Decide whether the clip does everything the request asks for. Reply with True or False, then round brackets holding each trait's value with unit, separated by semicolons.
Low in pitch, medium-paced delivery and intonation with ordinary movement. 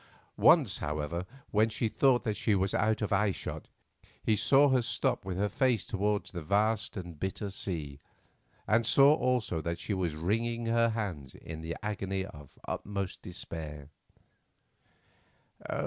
True (100 Hz; 150 wpm; 4.7 semitones)